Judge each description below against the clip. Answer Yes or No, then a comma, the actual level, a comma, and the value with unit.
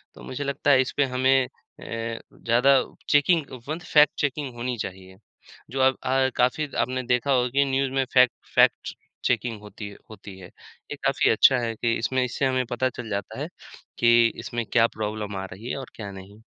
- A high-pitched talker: No, low, 125 Hz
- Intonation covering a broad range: No, average, 2.8 semitones